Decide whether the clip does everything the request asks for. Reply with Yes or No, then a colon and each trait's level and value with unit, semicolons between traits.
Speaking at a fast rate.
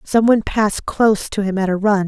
Yes: fast, 260 wpm